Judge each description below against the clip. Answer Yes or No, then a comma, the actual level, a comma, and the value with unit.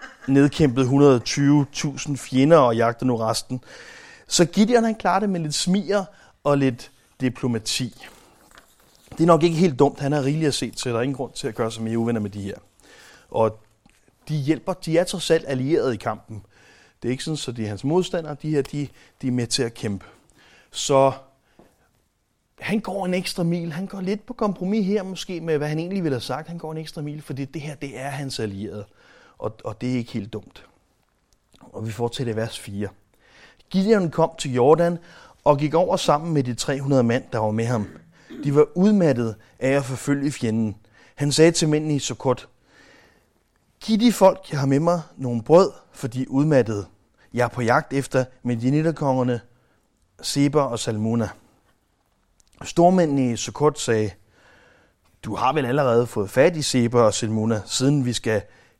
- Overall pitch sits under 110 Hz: No, medium, 140 Hz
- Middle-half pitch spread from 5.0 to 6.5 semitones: Yes, wide, 5.6 semitones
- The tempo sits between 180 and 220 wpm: Yes, average, 190 wpm